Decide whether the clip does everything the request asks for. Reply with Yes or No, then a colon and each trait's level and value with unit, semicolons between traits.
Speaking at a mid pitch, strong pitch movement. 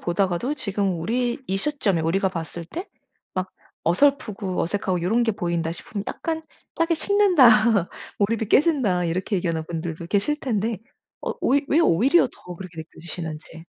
No: high, 195 Hz; wide, 6.6 semitones